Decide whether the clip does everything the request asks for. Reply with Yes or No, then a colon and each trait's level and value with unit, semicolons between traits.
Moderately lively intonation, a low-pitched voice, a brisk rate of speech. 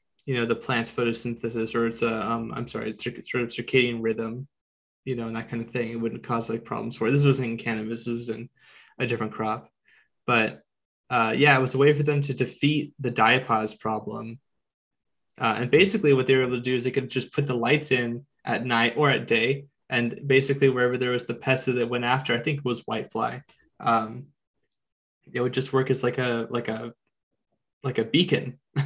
No: narrow, 2.3 semitones; low, 125 Hz; fast, 220 wpm